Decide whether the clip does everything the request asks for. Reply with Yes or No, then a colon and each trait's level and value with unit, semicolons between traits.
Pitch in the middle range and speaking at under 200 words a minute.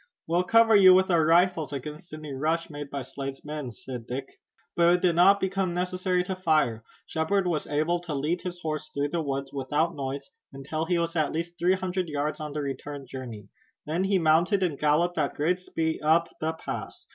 No: medium, 160 Hz; fast, 205 wpm